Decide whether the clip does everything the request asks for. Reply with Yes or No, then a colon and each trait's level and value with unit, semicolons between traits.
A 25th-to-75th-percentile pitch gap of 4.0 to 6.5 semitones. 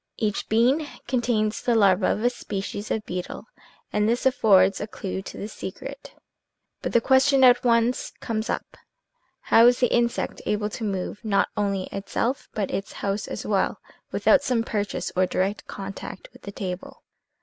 No: average, 3.4 semitones